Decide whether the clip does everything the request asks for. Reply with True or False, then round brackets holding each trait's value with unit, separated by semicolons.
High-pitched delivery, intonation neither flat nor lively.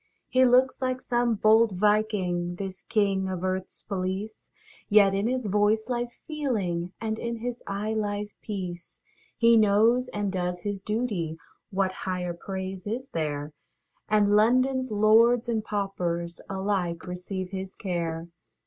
True (205 Hz; 3.4 semitones)